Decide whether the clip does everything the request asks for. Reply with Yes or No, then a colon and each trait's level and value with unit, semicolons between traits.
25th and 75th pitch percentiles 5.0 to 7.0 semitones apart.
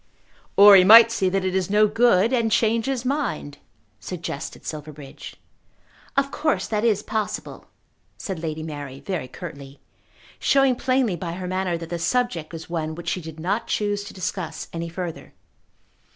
Yes: wide, 5.4 semitones